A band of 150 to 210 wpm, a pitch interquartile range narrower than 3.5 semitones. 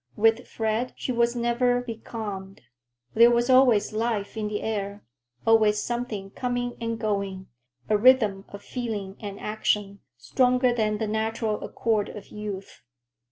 No: slow, 135 wpm; average, 2.7 semitones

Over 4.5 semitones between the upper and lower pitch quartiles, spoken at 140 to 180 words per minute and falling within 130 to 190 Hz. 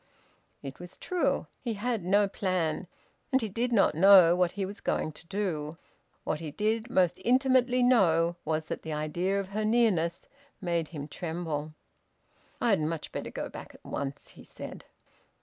Yes: average, 5.1 semitones; average, 165 wpm; medium, 185 Hz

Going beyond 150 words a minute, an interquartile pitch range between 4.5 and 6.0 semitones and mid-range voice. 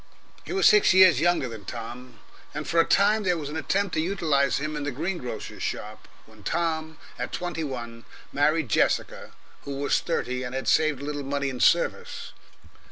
Yes: average, 190 wpm; average, 4.9 semitones; medium, 150 Hz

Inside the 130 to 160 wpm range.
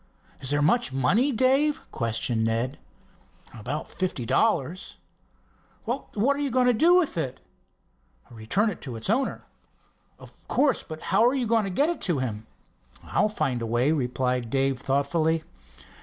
Yes: average, 155 wpm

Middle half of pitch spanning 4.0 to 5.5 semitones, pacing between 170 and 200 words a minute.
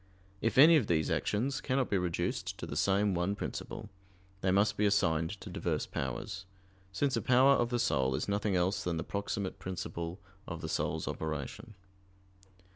Yes: average, 4.4 semitones; average, 175 wpm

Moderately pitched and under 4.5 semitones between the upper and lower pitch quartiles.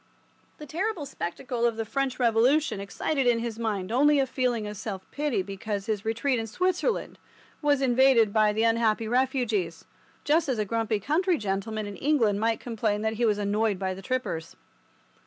No: high, 230 Hz; average, 4.1 semitones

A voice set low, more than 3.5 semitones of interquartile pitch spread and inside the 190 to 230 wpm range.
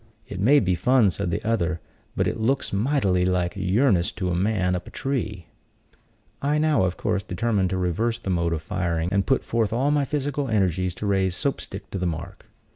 Yes: low, 100 Hz; average, 4.6 semitones; fast, 205 wpm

